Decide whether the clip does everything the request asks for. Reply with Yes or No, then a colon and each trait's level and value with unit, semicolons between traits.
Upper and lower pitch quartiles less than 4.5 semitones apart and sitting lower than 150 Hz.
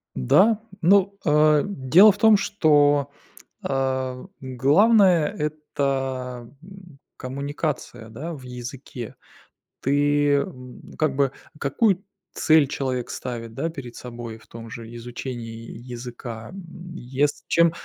No: average, 4.8 semitones; medium, 140 Hz